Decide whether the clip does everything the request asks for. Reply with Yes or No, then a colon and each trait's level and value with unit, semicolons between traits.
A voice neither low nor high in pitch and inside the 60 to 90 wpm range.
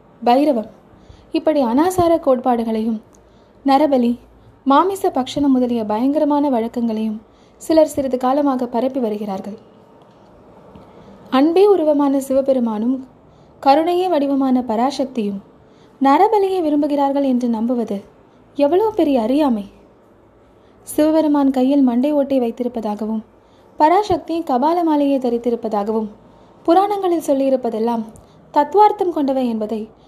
No: very high, 270 Hz; average, 80 wpm